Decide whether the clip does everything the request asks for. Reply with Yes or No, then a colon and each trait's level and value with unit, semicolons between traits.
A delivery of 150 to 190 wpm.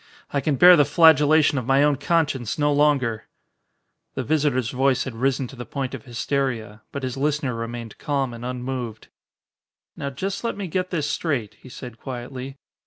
Yes: average, 175 wpm